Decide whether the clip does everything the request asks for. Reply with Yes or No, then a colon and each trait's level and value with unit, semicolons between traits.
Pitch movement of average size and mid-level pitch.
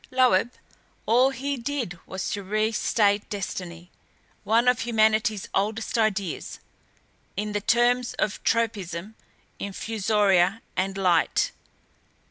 No: average, 3.1 semitones; high, 215 Hz